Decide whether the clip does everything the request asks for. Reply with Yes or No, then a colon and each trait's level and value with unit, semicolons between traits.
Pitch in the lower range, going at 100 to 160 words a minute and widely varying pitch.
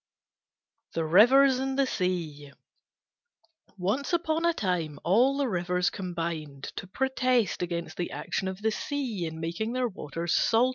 No: high, 190 Hz; average, 145 wpm; wide, 7.1 semitones